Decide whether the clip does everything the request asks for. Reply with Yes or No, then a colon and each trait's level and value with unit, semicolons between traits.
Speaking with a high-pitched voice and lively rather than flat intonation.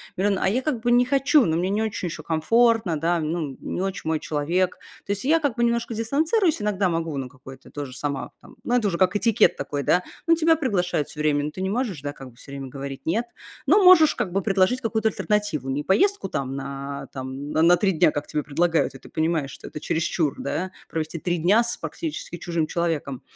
No: medium, 175 Hz; wide, 7.2 semitones